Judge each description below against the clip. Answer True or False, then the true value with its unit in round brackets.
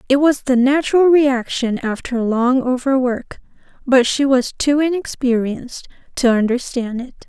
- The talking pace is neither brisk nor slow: False (130 wpm)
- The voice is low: False (260 Hz)